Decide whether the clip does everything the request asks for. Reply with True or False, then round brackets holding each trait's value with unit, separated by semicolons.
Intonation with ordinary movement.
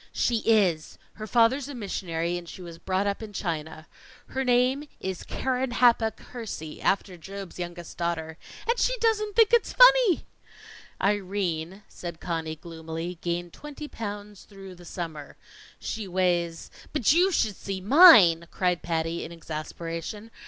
False (5.9 semitones)